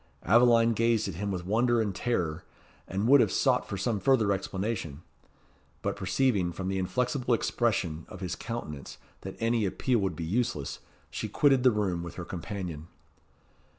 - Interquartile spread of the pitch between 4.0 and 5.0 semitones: Yes, average, 4.7 semitones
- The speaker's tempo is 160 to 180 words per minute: Yes, average, 165 wpm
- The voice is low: Yes, low, 100 Hz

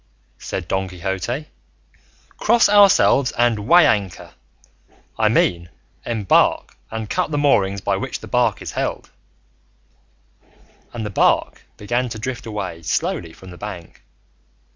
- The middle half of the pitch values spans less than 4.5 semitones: No, average, 4.9 semitones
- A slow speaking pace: Yes, slow, 130 wpm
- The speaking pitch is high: No, low, 105 Hz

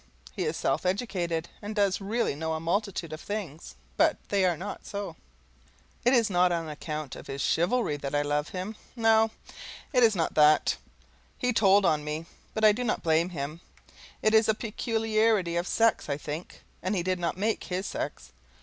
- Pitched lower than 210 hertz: Yes, medium, 185 Hz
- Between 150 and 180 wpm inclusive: No, average, 190 wpm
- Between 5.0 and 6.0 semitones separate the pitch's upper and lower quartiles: Yes, average, 5.3 semitones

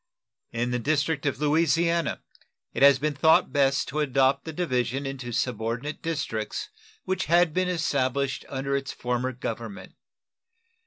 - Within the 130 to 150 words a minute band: Yes, average, 140 wpm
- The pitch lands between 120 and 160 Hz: Yes, medium, 140 Hz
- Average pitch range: Yes, average, 3.6 semitones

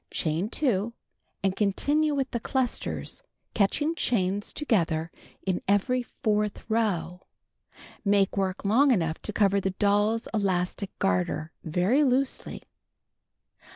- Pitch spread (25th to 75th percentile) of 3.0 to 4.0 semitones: No, average, 4.5 semitones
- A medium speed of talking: No, slow, 115 wpm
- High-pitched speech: Yes, high, 205 Hz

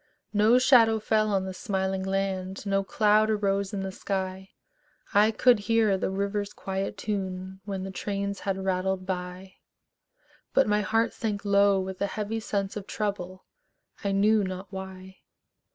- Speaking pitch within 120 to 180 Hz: No, high, 195 Hz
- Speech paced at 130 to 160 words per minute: Yes, average, 155 wpm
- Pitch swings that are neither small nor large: No, narrow, 1.6 semitones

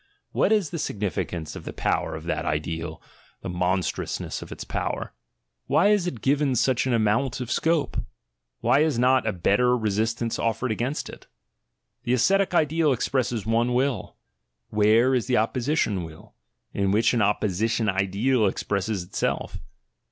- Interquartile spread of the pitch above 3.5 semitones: Yes, average, 4.6 semitones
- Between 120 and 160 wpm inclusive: Yes, average, 155 wpm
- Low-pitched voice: Yes, low, 115 Hz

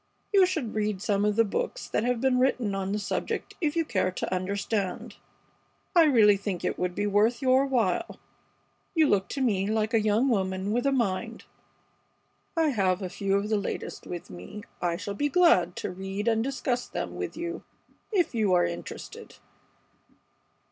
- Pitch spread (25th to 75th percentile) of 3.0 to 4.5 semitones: No, average, 5.0 semitones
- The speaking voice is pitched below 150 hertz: No, high, 210 Hz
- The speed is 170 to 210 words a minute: Yes, average, 180 wpm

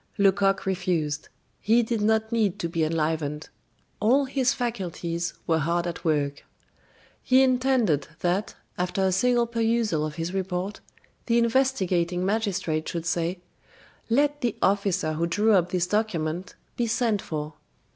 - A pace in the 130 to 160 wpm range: Yes, average, 140 wpm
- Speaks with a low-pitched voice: No, high, 190 Hz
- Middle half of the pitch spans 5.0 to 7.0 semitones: Yes, average, 5.3 semitones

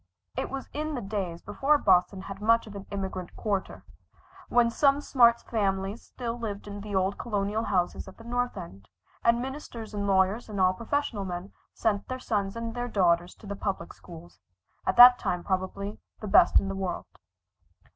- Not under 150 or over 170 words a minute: No, average, 185 wpm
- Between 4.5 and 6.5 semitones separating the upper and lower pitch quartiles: No, average, 3.5 semitones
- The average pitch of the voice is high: Yes, high, 205 Hz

